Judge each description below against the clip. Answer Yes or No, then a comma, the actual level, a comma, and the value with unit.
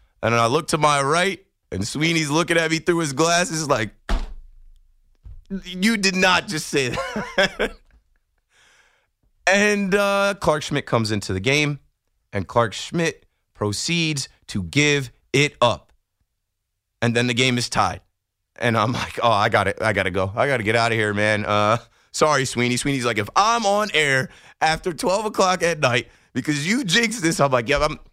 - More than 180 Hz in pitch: No, low, 135 Hz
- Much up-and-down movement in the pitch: Yes, wide, 7.6 semitones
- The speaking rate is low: No, average, 175 wpm